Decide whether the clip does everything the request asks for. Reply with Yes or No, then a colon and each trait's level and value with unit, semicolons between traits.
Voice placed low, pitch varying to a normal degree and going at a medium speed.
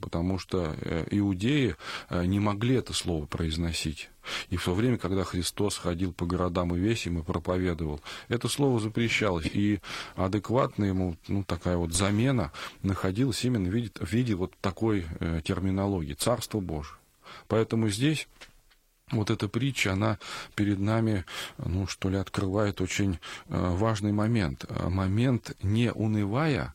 Yes: low, 100 Hz; average, 3.9 semitones; average, 135 wpm